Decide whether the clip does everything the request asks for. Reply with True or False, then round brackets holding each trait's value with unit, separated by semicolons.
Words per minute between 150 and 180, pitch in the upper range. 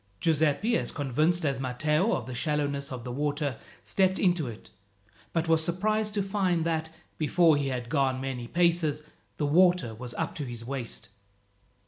False (165 wpm; 150 Hz)